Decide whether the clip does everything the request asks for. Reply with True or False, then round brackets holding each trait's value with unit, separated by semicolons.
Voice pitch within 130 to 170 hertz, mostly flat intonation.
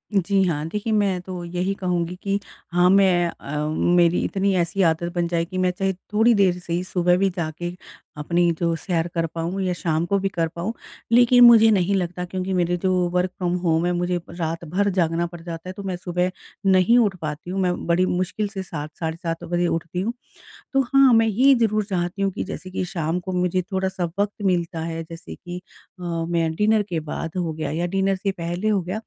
False (180 Hz; 2.3 semitones)